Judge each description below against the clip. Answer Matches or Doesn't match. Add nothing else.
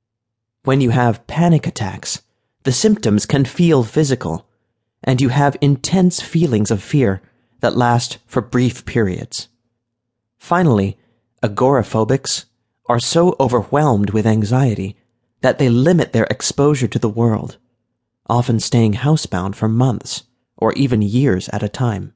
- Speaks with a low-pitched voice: Matches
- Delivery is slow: Matches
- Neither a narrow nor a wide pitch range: Matches